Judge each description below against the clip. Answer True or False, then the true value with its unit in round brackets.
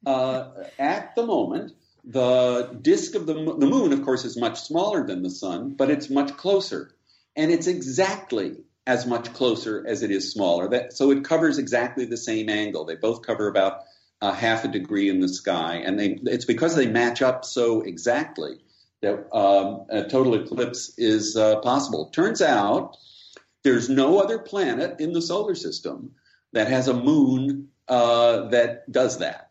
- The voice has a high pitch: False (135 Hz)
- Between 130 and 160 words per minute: False (175 wpm)